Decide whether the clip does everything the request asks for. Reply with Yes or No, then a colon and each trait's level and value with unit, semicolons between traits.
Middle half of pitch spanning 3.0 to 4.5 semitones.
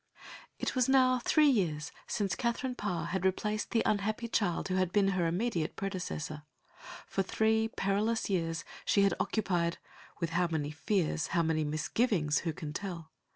No: average, 4.9 semitones